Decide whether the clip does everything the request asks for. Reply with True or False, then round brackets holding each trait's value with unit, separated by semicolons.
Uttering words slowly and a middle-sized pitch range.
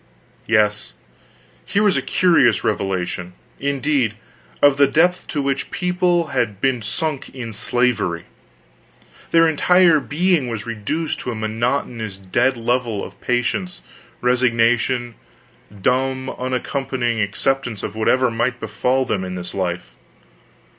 True (125 wpm; 4.3 semitones)